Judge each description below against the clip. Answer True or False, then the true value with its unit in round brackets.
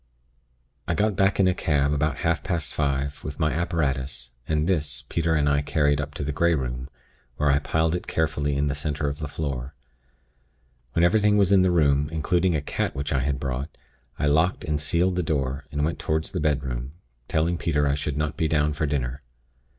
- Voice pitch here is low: True (75 Hz)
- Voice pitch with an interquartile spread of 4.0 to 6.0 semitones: False (2.6 semitones)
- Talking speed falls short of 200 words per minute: False (205 wpm)